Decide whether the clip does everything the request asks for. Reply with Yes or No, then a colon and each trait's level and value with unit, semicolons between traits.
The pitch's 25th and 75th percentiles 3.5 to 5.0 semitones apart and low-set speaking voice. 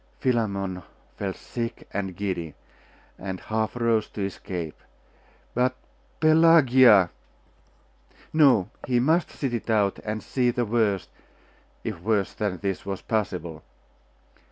Yes: average, 4.1 semitones; low, 110 Hz